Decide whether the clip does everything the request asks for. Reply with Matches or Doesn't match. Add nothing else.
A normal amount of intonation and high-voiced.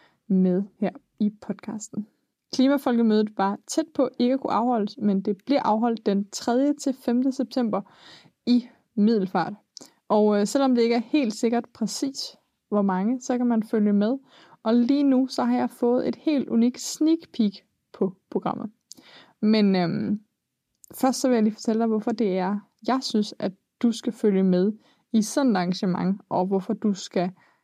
Matches